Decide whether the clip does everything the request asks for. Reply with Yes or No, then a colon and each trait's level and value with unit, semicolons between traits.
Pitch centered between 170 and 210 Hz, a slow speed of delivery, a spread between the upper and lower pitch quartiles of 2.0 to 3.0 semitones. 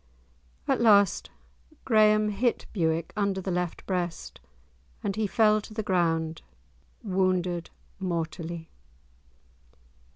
No: medium, 185 Hz; slow, 100 wpm; average, 3.7 semitones